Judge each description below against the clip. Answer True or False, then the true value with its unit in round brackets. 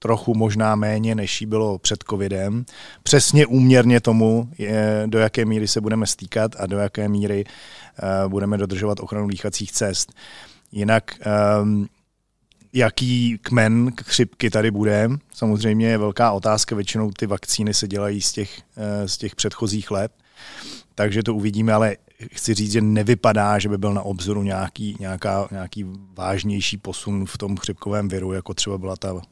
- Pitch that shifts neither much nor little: False (1.9 semitones)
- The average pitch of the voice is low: True (105 Hz)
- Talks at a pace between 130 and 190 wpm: True (150 wpm)